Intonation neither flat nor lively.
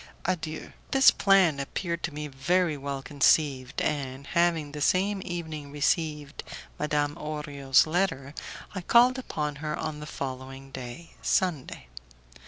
Yes: average, 3.6 semitones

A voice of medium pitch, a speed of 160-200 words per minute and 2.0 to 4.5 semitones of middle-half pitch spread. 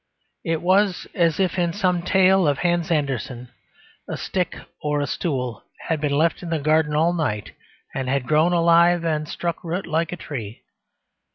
Yes: medium, 165 Hz; average, 175 wpm; average, 3.1 semitones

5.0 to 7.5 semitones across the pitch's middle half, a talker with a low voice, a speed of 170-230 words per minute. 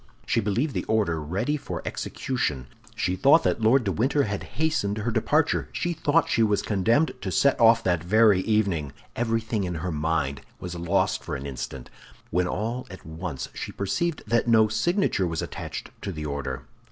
Yes: wide, 5.5 semitones; low, 105 Hz; average, 180 wpm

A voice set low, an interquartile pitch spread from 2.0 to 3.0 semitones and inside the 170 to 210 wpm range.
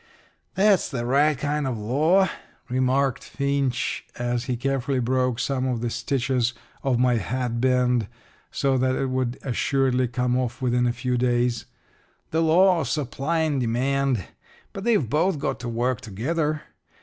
No: low, 130 Hz; narrow, 2.4 semitones; average, 155 wpm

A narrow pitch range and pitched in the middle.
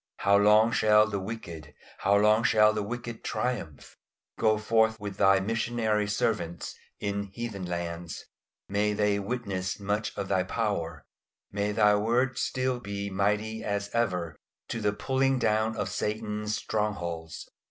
No: narrow, 2.0 semitones; low, 105 Hz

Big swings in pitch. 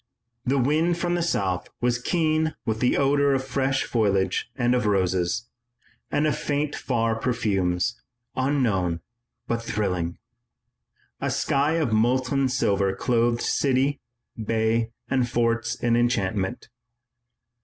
No: average, 4.3 semitones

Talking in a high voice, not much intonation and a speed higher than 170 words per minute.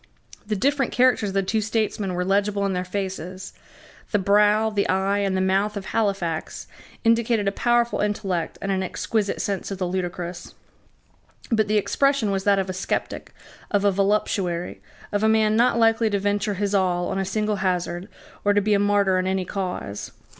Yes: high, 200 Hz; narrow, 2.1 semitones; average, 190 wpm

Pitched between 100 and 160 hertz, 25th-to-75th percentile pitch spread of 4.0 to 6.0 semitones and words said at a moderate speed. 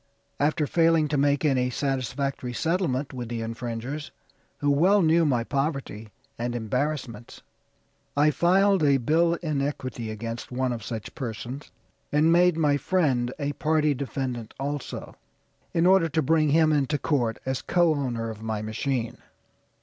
Yes: medium, 140 Hz; average, 4.3 semitones; average, 150 wpm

